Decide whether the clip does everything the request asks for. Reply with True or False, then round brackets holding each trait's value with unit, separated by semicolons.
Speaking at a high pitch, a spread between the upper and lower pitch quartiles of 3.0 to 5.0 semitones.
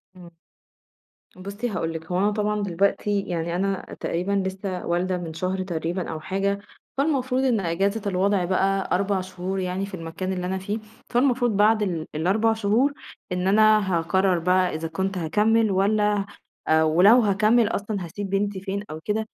False (195 Hz; 2.5 semitones)